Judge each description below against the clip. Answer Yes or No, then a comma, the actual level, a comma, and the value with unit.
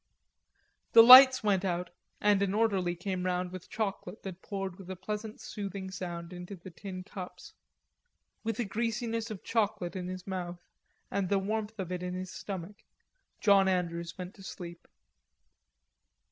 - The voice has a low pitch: No, high, 190 Hz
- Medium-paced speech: Yes, average, 160 wpm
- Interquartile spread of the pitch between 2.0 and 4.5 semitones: Yes, narrow, 2.6 semitones